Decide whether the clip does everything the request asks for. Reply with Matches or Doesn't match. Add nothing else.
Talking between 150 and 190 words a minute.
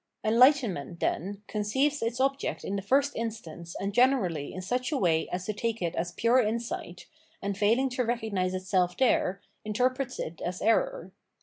Matches